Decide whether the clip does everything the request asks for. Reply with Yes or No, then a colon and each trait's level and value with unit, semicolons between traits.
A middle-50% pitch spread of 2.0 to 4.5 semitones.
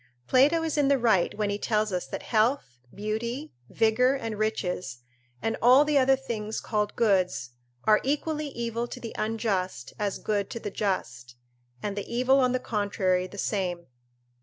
Yes: average, 4.2 semitones